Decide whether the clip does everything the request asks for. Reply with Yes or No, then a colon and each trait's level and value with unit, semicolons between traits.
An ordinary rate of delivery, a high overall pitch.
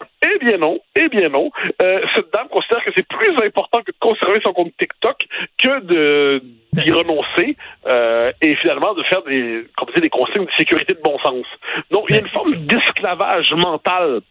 Yes: average, 195 wpm; high, 195 Hz